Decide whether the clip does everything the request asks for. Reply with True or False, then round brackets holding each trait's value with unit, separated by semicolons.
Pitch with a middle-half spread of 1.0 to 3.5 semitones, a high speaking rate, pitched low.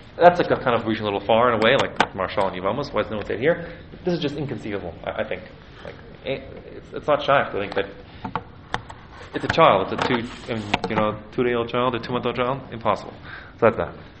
True (3.0 semitones; 240 wpm; 115 Hz)